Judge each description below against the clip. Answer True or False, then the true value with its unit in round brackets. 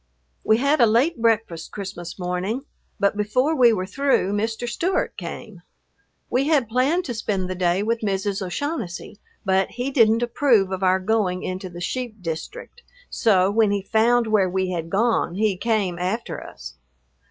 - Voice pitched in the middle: False (215 Hz)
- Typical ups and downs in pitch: True (4.4 semitones)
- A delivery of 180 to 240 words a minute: False (165 wpm)